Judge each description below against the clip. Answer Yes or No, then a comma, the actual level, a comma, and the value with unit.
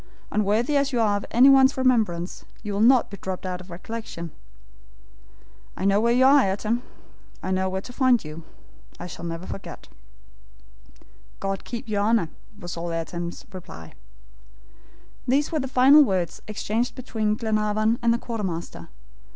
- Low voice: No, high, 215 Hz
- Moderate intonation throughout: Yes, average, 4.7 semitones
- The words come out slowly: No, average, 155 wpm